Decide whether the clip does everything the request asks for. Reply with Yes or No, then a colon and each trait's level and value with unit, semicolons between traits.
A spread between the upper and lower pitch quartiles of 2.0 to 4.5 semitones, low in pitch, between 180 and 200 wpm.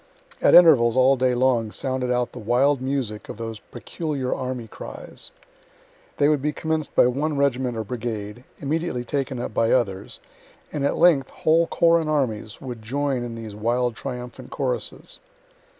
No: average, 3.3 semitones; low, 125 Hz; average, 165 wpm